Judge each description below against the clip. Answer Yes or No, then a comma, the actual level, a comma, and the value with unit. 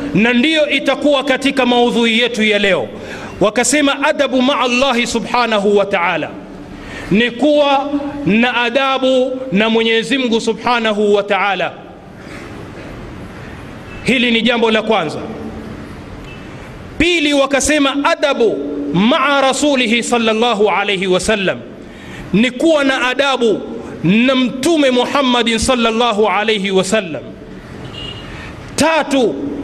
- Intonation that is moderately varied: Yes, average, 3.8 semitones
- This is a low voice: No, high, 245 Hz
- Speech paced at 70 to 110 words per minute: Yes, slow, 100 wpm